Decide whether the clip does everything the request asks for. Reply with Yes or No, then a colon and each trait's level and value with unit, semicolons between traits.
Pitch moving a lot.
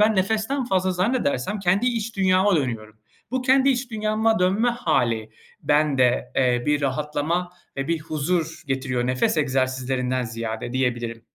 Yes: wide, 8.6 semitones